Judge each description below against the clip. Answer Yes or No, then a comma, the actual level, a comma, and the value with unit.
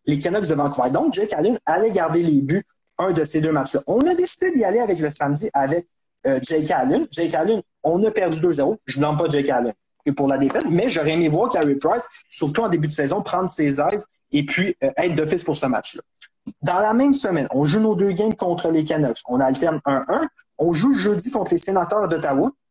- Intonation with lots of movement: Yes, wide, 6.3 semitones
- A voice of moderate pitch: Yes, medium, 165 Hz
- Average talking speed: No, fast, 230 wpm